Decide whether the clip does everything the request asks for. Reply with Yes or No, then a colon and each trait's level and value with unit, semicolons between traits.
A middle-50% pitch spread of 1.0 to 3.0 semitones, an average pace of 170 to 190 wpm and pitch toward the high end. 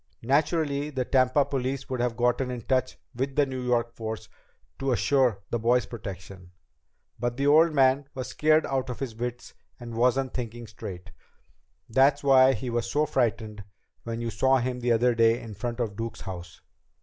No: average, 2.7 semitones; average, 175 wpm; low, 125 Hz